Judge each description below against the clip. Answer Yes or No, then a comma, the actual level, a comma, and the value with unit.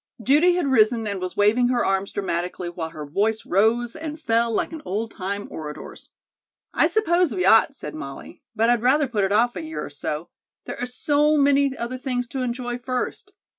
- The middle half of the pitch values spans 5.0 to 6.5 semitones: Yes, wide, 5.6 semitones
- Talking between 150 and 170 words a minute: No, average, 200 wpm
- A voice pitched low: No, high, 235 Hz